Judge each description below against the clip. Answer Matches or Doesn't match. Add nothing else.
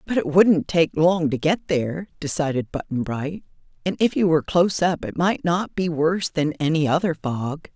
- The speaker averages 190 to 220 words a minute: Matches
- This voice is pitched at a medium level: Matches